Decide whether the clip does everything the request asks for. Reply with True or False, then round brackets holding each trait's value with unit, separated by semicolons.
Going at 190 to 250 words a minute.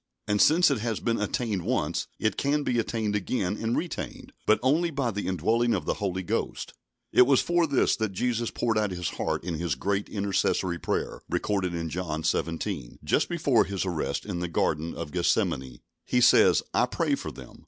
True (195 wpm)